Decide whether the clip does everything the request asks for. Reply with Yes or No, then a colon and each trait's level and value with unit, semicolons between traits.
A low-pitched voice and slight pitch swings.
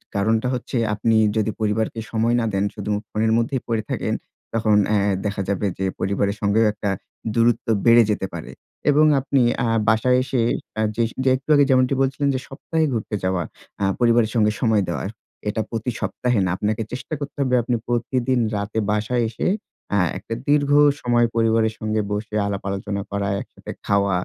No: low, 110 Hz; average, 3.0 semitones